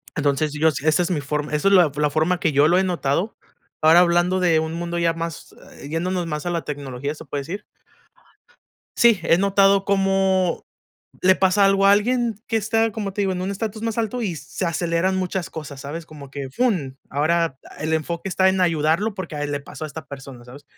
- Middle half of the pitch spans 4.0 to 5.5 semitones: Yes, average, 4.3 semitones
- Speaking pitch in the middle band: Yes, medium, 170 Hz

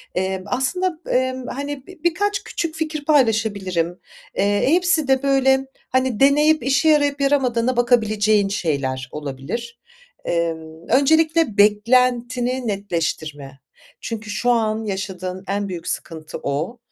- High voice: Yes, high, 235 Hz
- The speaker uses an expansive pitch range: Yes, wide, 6.5 semitones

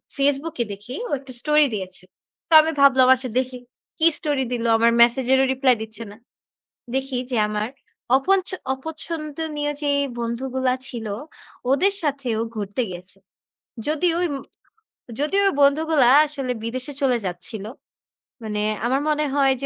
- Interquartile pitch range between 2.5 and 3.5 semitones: No, average, 4.0 semitones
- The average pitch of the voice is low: No, very high, 265 Hz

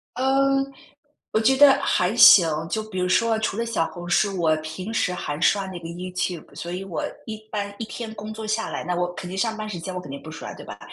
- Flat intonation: No, average, 3.9 semitones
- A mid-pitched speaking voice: No, high, 195 Hz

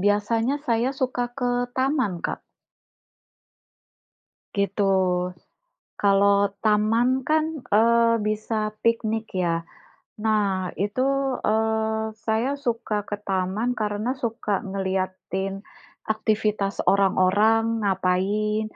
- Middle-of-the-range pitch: No, high, 215 Hz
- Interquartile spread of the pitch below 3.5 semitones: Yes, narrow, 2.6 semitones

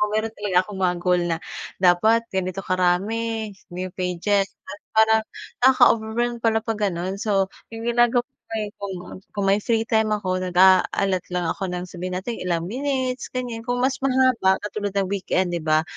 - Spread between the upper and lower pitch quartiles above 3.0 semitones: Yes, average, 3.7 semitones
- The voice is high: Yes, high, 200 Hz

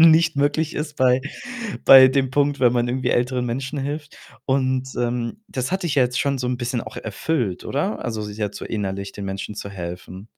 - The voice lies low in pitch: Yes, low, 125 Hz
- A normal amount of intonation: Yes, average, 4.0 semitones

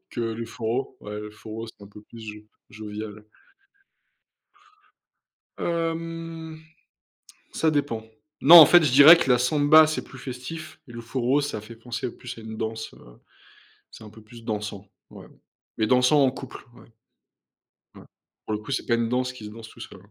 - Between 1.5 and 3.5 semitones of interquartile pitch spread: No, average, 4.7 semitones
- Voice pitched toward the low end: Yes, low, 120 Hz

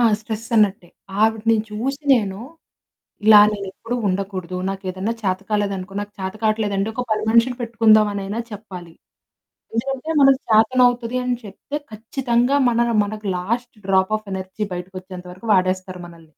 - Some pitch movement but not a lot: Yes, average, 3.4 semitones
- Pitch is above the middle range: Yes, high, 210 Hz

